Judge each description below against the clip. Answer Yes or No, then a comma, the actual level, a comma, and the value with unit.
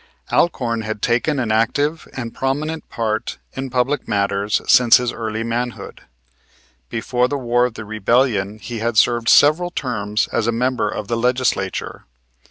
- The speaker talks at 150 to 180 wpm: Yes, average, 155 wpm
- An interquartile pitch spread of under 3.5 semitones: Yes, average, 2.8 semitones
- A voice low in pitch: Yes, low, 120 Hz